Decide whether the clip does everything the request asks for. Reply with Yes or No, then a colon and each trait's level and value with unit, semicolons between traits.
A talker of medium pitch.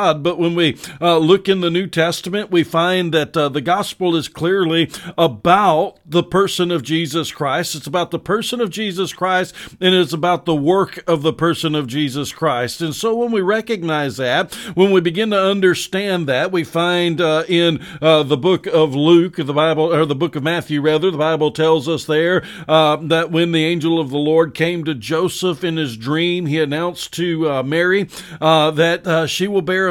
Yes: medium, 165 Hz